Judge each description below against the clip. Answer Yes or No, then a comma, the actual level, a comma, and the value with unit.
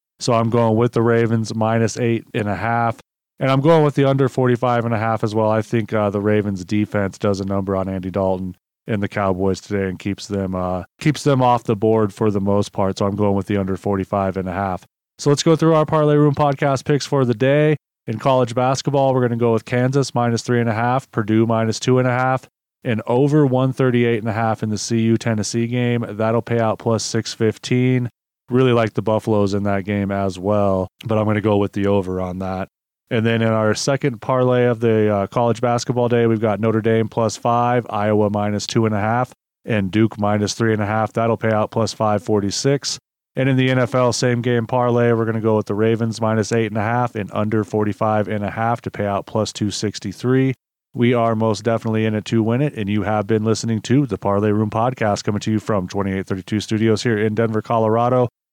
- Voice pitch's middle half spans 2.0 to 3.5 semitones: Yes, average, 2.8 semitones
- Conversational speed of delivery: No, fast, 235 wpm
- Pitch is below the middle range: Yes, low, 110 Hz